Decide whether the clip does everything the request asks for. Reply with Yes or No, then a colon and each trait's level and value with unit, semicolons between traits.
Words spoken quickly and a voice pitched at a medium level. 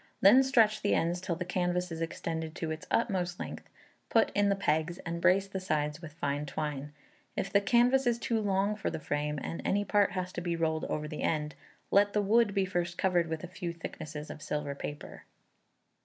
Yes: fast, 210 wpm; medium, 175 Hz